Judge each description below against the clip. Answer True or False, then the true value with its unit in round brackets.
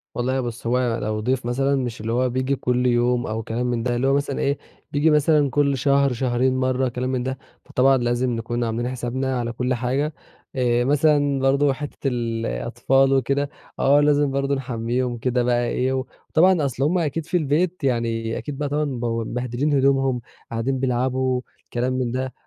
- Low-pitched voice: True (130 Hz)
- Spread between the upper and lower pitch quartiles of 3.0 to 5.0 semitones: False (2.4 semitones)